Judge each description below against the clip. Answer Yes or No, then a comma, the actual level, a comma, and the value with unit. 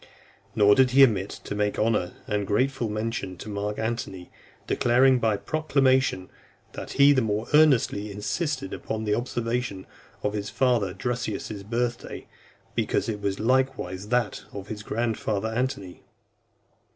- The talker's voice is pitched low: Yes, low, 110 Hz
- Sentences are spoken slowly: No, average, 145 wpm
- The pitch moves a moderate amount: Yes, average, 3.4 semitones